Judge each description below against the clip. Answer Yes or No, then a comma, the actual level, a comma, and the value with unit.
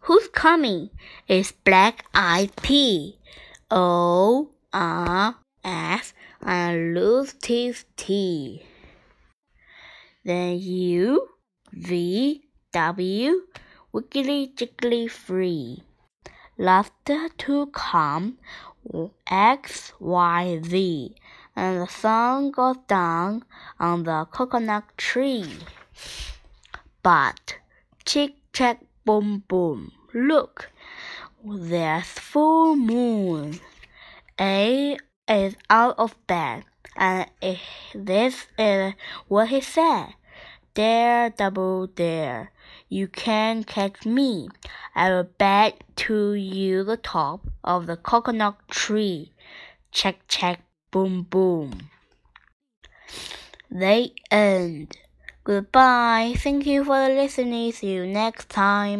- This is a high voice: Yes, high, 205 Hz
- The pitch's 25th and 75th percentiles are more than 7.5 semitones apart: No, wide, 5.4 semitones